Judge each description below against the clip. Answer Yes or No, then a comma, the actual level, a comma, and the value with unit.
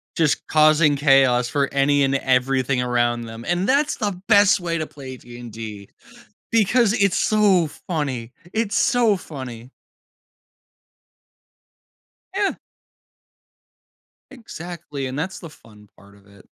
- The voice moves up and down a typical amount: No, wide, 7.2 semitones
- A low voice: No, medium, 145 Hz